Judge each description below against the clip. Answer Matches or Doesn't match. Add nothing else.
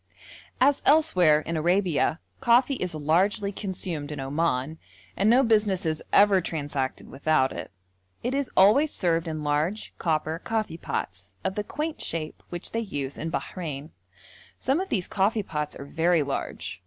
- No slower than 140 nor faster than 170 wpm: Matches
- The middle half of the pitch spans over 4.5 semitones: Matches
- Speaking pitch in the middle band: Matches